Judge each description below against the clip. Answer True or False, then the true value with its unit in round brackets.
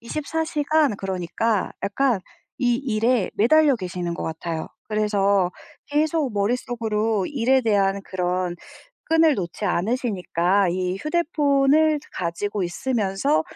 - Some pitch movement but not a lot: False (6.6 semitones)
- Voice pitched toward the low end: False (215 Hz)